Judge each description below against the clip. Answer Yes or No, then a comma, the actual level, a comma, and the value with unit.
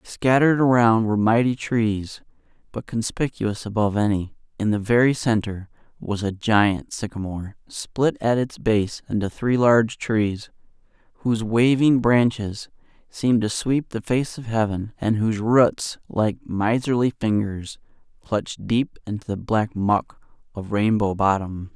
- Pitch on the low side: Yes, low, 110 Hz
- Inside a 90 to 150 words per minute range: Yes, average, 140 wpm